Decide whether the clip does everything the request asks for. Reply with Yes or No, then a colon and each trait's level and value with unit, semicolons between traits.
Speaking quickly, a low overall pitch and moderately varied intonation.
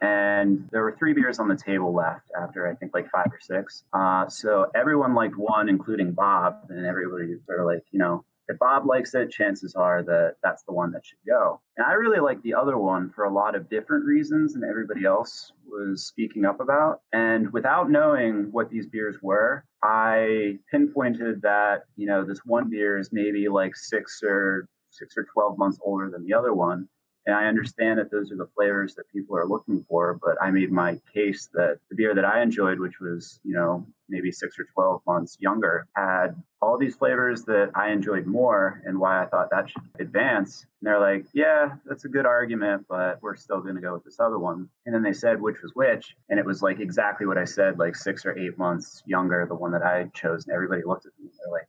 Yes: fast, 225 wpm; low, 100 Hz; average, 3.4 semitones